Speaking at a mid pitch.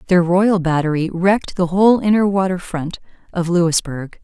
Yes: medium, 180 Hz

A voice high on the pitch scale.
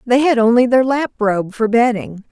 Yes: high, 235 Hz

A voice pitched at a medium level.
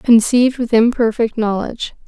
No: high, 230 Hz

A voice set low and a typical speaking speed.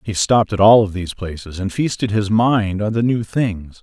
No: low, 105 Hz; fast, 235 wpm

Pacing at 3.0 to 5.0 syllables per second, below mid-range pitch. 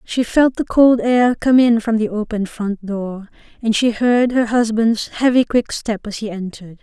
No: 4.6 syllables/s; high, 225 Hz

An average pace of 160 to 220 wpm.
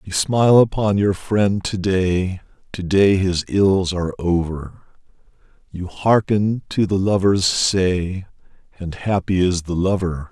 No: average, 140 wpm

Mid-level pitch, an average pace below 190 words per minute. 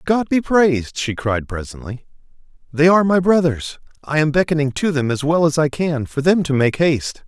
No: medium, 150 Hz; fast, 205 wpm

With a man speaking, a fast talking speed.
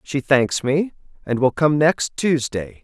No: male; average, 170 wpm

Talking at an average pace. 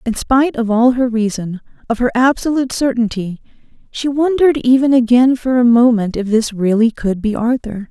Yes: average, 175 wpm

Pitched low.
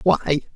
No: medium, 160 Hz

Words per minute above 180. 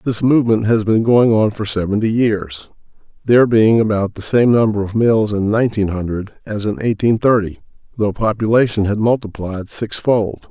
No: average, 170 wpm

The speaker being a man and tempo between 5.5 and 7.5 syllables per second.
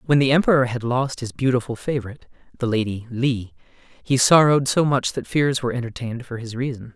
Yes: male; 5.8 syllables/s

